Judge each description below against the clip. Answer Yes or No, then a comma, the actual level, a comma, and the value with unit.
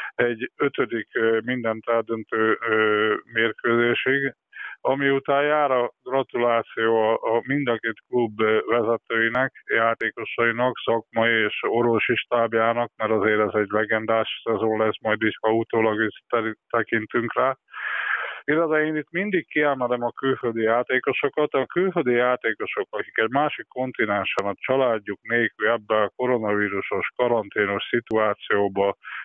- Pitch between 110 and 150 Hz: Yes, low, 115 Hz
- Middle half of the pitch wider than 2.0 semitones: Yes, narrow, 2.4 semitones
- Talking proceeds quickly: No, average, 120 wpm